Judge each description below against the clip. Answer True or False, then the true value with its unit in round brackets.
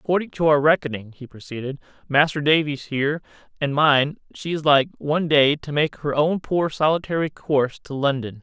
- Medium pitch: True (150 Hz)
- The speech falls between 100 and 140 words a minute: False (180 wpm)